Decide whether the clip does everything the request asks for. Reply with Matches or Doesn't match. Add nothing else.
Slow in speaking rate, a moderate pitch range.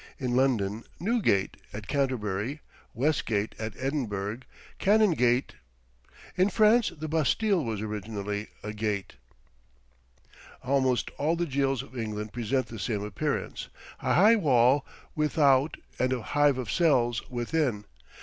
Doesn't match